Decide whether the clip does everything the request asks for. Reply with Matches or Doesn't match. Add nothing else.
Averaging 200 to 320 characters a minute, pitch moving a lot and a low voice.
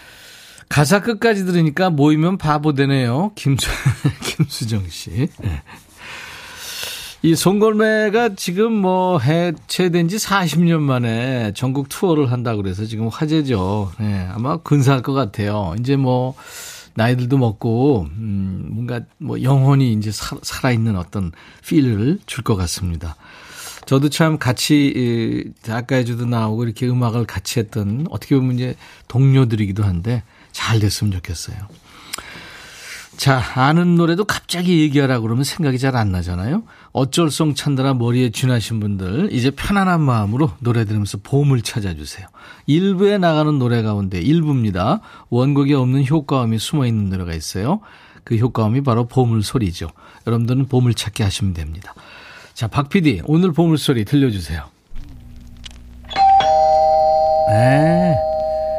Matches